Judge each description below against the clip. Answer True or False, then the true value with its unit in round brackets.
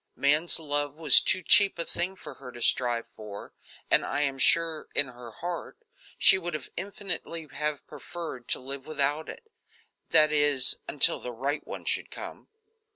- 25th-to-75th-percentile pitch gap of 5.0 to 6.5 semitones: False (3.8 semitones)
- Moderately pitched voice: True (150 Hz)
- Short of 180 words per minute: True (165 wpm)